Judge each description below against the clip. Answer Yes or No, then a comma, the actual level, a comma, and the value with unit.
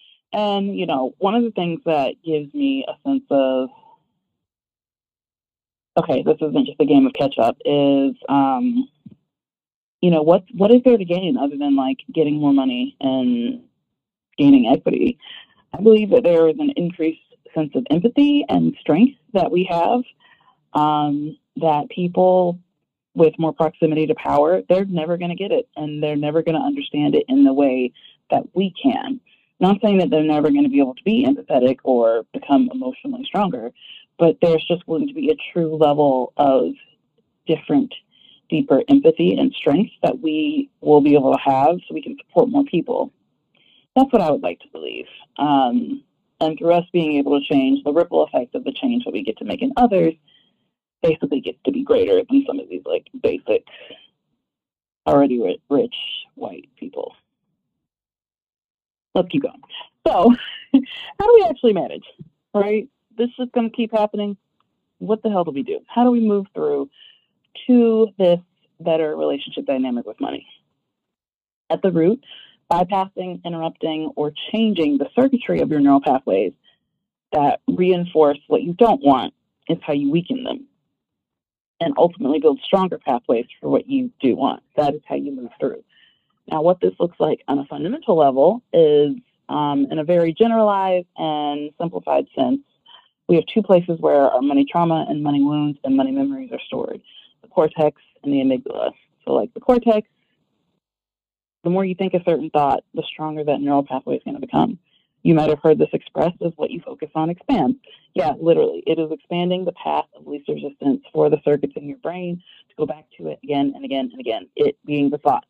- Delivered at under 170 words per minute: No, average, 180 wpm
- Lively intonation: Yes, wide, 8.8 semitones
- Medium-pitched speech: Yes, medium, 175 Hz